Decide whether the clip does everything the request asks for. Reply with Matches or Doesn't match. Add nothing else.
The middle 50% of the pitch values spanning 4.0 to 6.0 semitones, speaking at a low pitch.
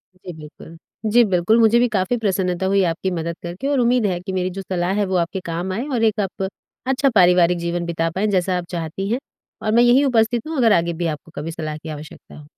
Doesn't match